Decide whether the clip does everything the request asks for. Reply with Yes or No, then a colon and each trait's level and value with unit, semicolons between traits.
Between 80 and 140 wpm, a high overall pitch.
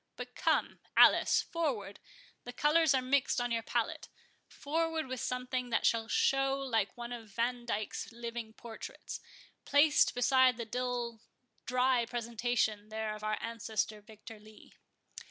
Yes: slow, 135 wpm; high, 240 Hz